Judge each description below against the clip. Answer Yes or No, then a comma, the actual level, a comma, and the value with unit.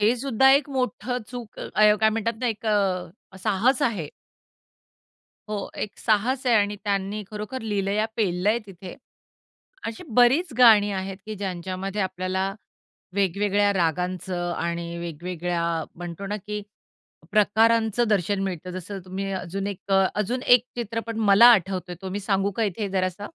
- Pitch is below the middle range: No, high, 200 Hz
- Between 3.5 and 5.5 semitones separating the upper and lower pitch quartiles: No, average, 3.1 semitones